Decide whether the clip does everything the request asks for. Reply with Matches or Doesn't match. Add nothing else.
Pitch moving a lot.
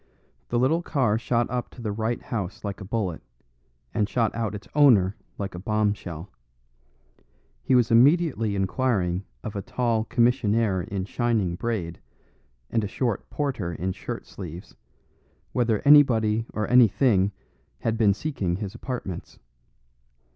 Doesn't match